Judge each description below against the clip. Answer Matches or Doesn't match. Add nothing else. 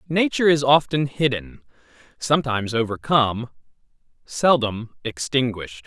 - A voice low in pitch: Matches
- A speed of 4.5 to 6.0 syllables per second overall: Matches